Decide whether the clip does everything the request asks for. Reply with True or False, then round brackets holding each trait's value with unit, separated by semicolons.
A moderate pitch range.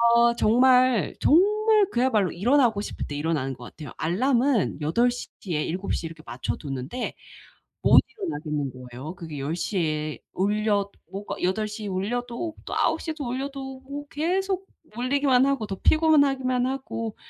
False (8.0 semitones)